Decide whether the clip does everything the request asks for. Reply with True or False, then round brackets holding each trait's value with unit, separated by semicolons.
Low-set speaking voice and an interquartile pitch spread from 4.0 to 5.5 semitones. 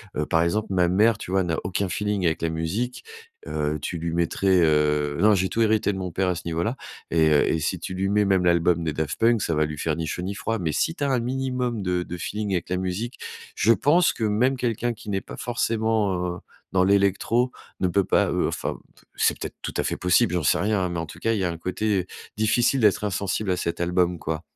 True (95 Hz; 4.3 semitones)